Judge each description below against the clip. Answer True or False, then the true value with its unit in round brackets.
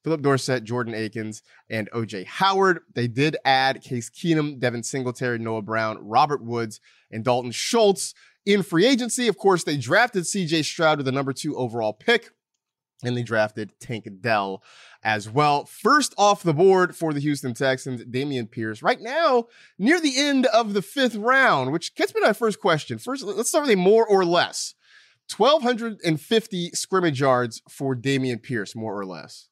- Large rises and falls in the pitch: True (8.9 semitones)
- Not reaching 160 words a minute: False (175 wpm)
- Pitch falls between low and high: True (145 Hz)